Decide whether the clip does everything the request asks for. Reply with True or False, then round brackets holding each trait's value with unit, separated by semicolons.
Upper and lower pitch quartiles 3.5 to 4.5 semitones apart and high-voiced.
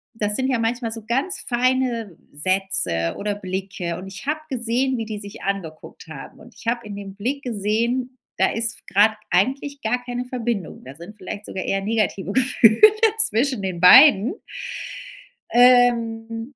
True (4.0 semitones; 225 Hz)